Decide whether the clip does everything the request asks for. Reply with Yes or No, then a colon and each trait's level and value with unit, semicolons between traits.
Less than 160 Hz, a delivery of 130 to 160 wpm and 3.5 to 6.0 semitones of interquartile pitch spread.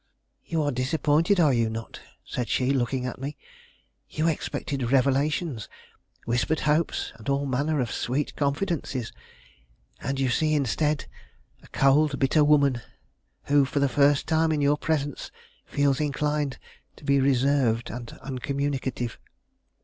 No: medium, 140 Hz; slow, 135 wpm; narrow, 2.5 semitones